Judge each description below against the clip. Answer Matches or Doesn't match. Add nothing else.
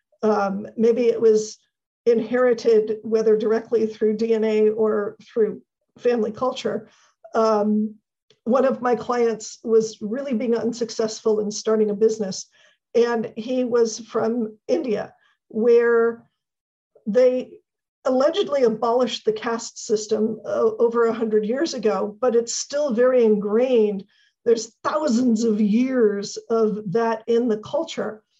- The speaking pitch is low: Doesn't match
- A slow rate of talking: Matches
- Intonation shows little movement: Matches